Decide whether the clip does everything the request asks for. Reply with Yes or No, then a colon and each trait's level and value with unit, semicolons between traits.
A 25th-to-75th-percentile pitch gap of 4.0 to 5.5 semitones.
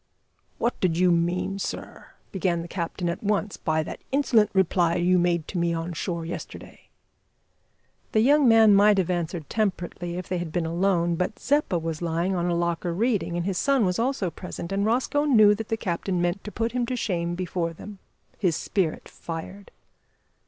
No: average, 3.5 semitones